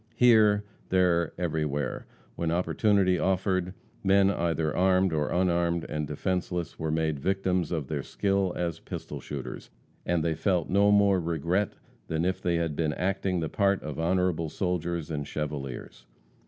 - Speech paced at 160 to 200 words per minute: No, average, 150 wpm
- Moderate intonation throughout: Yes, average, 3.0 semitones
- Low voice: Yes, very low, 85 Hz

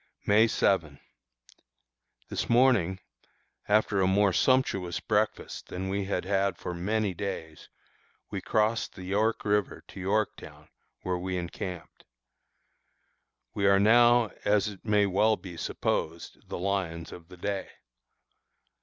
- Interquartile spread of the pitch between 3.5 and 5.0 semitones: No, average, 2.7 semitones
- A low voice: Yes, low, 100 Hz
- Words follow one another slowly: Yes, slow, 125 wpm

